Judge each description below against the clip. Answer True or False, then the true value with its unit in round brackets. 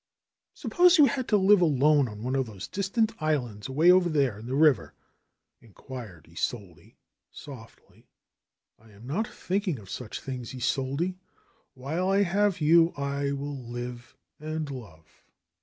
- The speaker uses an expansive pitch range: True (6.4 semitones)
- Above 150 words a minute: False (145 wpm)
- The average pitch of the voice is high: False (140 Hz)